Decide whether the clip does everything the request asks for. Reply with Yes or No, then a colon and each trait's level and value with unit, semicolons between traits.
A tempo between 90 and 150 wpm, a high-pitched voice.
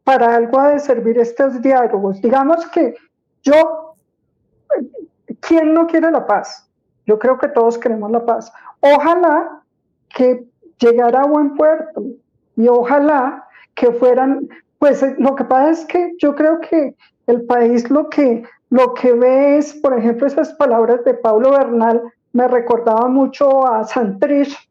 Yes: average, 145 wpm; very high, 270 Hz